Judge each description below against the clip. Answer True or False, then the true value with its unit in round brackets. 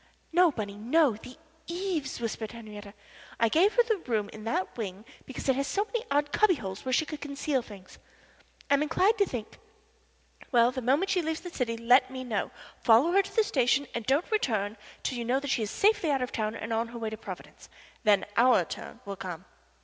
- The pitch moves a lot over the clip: True (6.2 semitones)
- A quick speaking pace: True (215 wpm)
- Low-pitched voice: False (255 Hz)